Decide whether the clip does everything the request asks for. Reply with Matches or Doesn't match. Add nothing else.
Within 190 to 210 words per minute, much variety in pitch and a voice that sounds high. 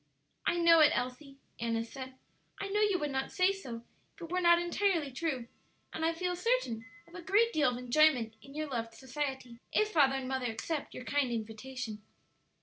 Matches